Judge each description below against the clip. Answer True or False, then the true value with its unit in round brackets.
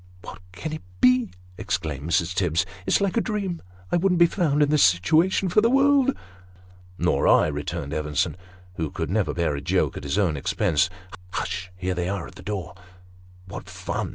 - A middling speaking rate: False (215 wpm)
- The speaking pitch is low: True (90 Hz)